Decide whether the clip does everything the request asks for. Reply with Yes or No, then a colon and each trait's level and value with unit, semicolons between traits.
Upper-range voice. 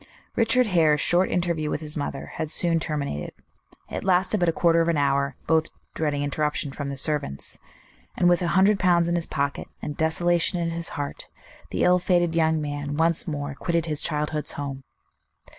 No: medium, 160 Hz